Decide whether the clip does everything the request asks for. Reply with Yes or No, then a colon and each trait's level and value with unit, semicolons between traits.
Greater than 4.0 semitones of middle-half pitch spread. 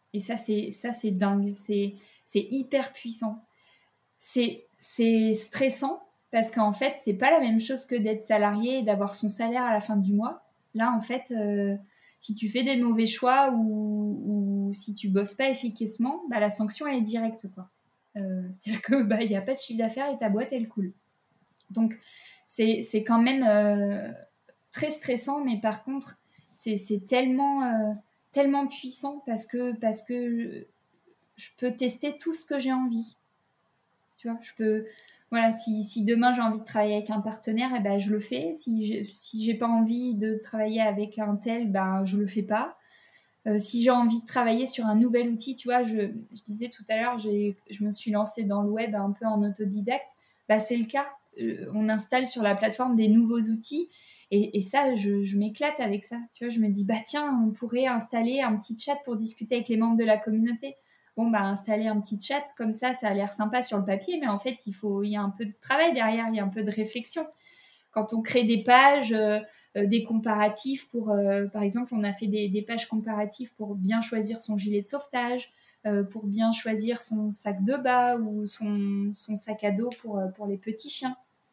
No: average, 2.8 semitones